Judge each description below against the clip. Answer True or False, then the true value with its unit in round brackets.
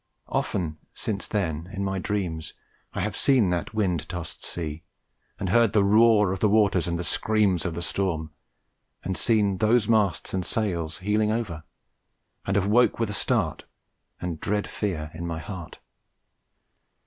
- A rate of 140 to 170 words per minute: True (160 wpm)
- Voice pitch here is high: False (95 Hz)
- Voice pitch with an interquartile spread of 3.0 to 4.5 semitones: True (3.8 semitones)